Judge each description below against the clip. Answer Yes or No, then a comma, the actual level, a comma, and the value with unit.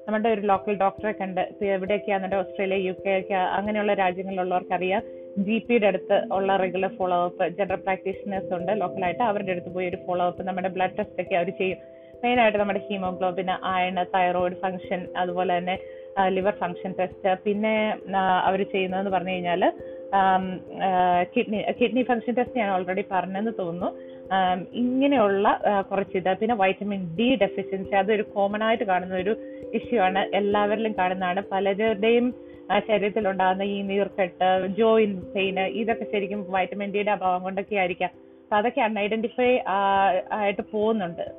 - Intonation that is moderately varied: No, narrow, 2.1 semitones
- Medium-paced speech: No, fast, 135 wpm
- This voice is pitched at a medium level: No, high, 195 Hz